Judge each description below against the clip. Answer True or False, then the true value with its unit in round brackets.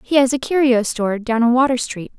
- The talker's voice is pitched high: True (245 Hz)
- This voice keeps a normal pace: False (245 wpm)